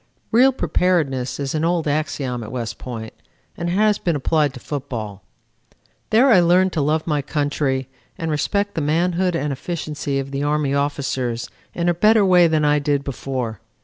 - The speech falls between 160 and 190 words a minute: Yes, average, 180 wpm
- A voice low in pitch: No, medium, 150 Hz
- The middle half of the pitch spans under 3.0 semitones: No, average, 4.1 semitones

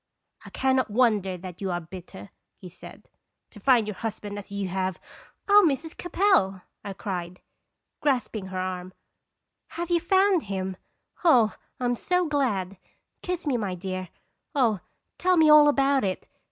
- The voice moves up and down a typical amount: No, wide, 7.7 semitones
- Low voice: No, high, 210 Hz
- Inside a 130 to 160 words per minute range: No, average, 170 wpm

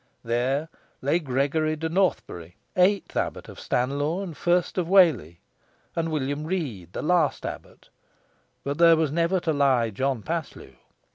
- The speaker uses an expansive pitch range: No, average, 4.3 semitones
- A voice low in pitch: No, medium, 155 Hz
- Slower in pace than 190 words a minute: Yes, average, 145 wpm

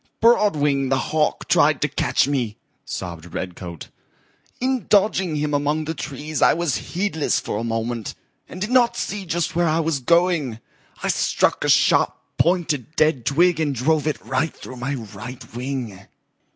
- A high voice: No, medium, 150 Hz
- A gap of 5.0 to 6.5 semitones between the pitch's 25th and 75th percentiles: Yes, wide, 5.5 semitones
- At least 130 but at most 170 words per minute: Yes, average, 165 wpm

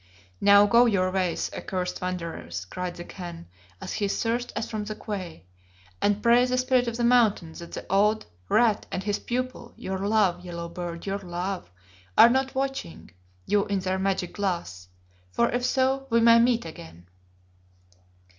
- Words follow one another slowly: No, average, 165 wpm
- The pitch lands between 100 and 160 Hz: No, high, 200 Hz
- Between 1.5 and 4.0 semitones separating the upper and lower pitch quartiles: No, average, 4.8 semitones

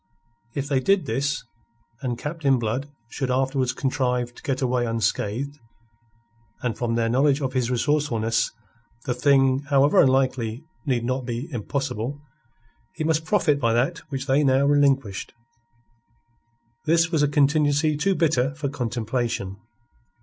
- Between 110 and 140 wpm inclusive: Yes, slow, 135 wpm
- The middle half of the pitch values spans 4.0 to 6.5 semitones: No, average, 3.1 semitones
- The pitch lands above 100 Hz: Yes, low, 135 Hz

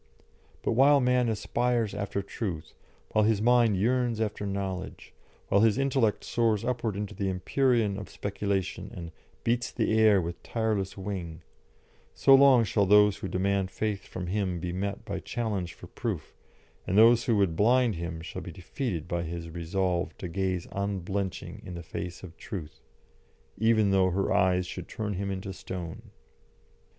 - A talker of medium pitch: No, low, 100 Hz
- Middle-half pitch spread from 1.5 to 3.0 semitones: No, average, 3.4 semitones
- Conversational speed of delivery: Yes, average, 160 wpm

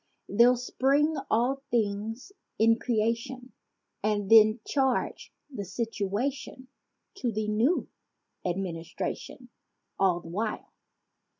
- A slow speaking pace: Yes, slow, 95 wpm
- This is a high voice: Yes, high, 225 Hz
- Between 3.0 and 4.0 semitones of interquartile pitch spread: Yes, average, 3.7 semitones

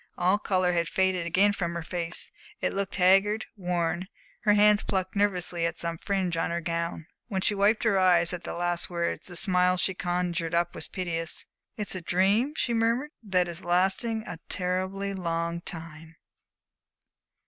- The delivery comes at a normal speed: Yes, average, 170 wpm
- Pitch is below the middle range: No, medium, 180 Hz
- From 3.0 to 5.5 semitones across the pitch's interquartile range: No, narrow, 2.5 semitones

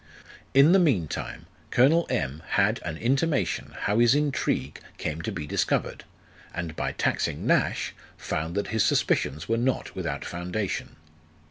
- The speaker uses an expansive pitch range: Yes, wide, 8.1 semitones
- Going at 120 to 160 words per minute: Yes, average, 145 wpm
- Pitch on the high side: No, low, 110 Hz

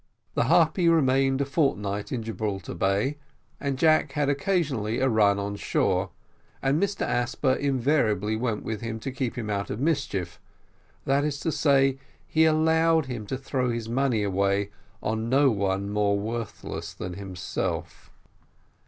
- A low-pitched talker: Yes, low, 120 Hz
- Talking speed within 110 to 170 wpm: Yes, average, 150 wpm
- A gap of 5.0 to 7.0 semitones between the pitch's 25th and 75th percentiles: Yes, wide, 5.4 semitones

